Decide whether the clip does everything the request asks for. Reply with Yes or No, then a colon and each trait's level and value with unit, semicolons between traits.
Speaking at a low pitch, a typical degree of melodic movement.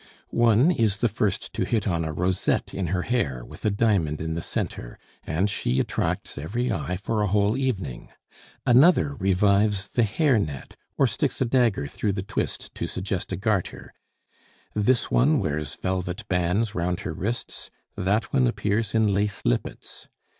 Yes: low, 100 Hz; average, 4.2 semitones